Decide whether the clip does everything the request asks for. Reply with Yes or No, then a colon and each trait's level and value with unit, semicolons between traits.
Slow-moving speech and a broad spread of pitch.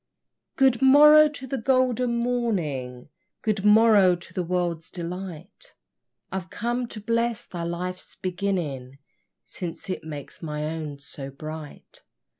Yes: slow, 125 wpm; wide, 6.8 semitones